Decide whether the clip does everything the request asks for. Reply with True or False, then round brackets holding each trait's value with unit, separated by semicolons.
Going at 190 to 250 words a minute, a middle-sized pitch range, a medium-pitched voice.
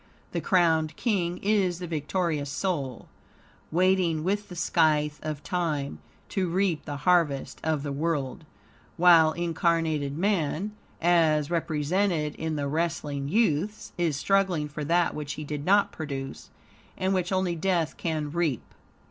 False (140 wpm; 3.2 semitones; 165 Hz)